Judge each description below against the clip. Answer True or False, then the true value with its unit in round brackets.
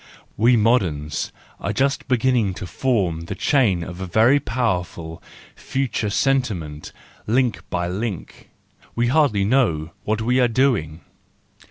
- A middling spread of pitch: False (6.3 semitones)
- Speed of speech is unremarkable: False (130 wpm)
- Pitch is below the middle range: True (110 Hz)